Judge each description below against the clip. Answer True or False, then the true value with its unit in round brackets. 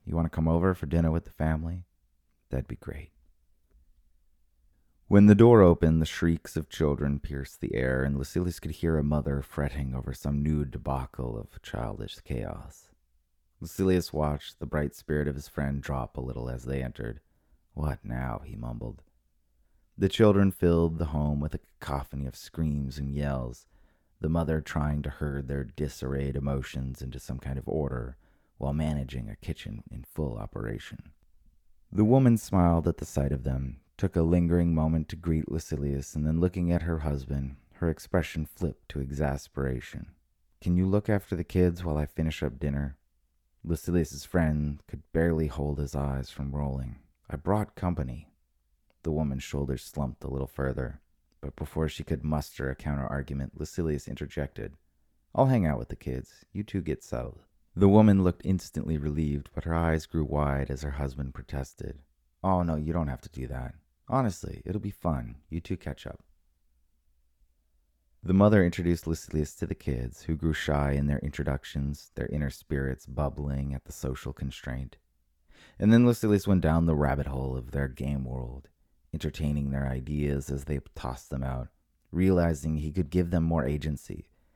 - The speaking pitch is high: False (75 Hz)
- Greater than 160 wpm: True (170 wpm)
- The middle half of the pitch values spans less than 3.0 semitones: False (3.5 semitones)